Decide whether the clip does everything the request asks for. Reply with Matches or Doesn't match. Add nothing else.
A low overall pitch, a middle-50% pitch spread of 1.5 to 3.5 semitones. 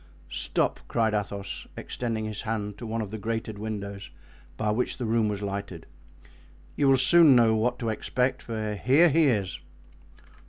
Matches